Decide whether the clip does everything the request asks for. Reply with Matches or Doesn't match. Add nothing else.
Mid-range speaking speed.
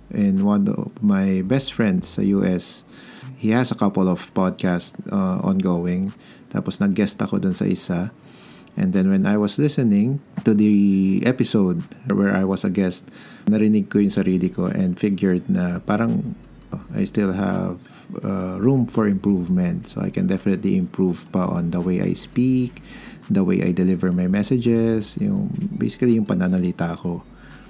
Doesn't match